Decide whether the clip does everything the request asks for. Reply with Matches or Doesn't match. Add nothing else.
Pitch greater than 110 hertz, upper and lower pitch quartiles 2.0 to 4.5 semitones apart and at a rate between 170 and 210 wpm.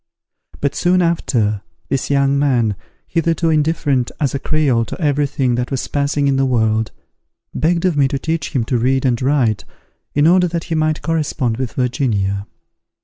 Matches